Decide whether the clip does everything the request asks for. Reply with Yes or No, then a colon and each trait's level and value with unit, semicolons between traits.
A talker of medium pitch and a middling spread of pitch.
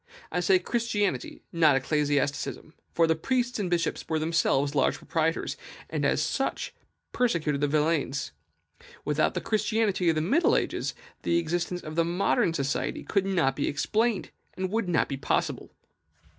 Yes: medium, 170 Hz; average, 4.6 semitones